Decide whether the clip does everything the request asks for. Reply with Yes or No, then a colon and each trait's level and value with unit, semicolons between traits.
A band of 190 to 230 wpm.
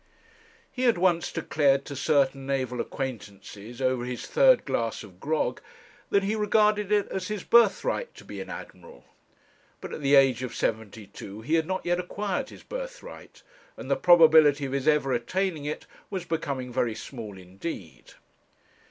No: average, 165 wpm